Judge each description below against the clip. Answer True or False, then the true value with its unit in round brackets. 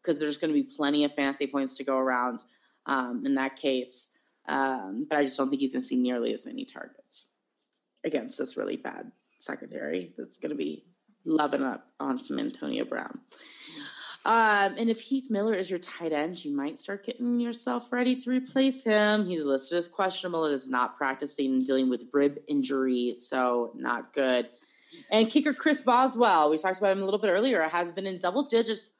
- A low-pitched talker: False (180 Hz)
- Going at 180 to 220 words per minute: True (200 wpm)